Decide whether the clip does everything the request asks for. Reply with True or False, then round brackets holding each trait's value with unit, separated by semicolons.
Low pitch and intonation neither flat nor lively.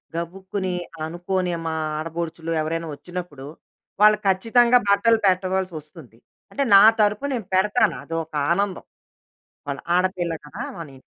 False (185 Hz; 3.4 semitones)